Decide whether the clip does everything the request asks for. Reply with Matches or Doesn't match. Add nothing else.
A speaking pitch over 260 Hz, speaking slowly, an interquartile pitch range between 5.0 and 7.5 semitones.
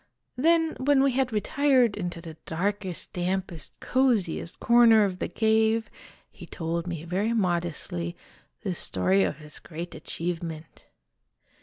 Doesn't match